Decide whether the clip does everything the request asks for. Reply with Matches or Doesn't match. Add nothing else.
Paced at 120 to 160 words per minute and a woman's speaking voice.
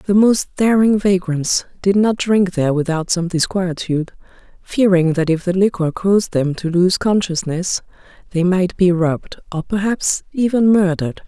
Matches